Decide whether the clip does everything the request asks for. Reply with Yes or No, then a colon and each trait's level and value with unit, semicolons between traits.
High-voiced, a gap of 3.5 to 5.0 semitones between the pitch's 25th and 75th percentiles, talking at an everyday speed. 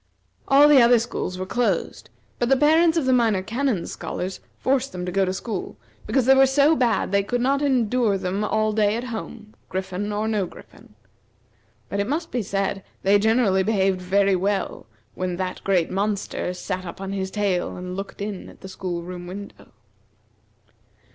Yes: high, 205 Hz; average, 4.4 semitones; average, 185 wpm